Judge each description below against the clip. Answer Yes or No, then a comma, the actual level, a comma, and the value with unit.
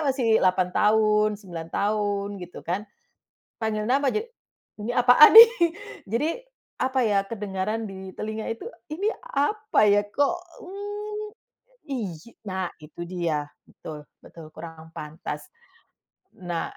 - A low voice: No, high, 210 Hz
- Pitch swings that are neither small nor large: No, wide, 6.5 semitones